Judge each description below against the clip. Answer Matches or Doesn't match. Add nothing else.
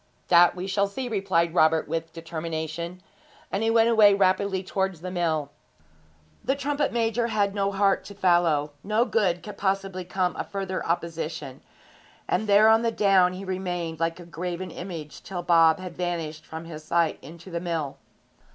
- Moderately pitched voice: Matches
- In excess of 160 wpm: Matches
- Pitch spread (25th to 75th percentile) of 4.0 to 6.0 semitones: Doesn't match